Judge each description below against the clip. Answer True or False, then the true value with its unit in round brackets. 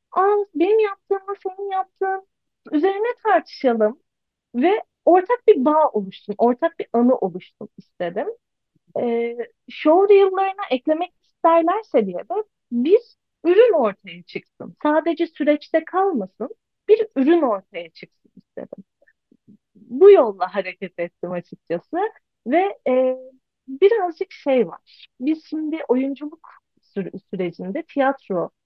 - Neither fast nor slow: True (110 wpm)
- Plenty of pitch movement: True (8.8 semitones)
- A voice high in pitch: True (310 Hz)